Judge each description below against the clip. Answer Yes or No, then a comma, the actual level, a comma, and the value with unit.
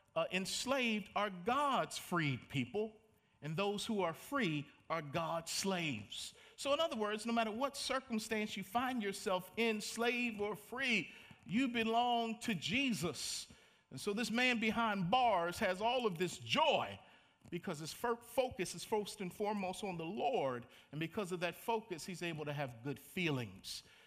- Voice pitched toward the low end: No, high, 200 Hz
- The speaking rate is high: No, average, 160 wpm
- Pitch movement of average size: No, wide, 5.7 semitones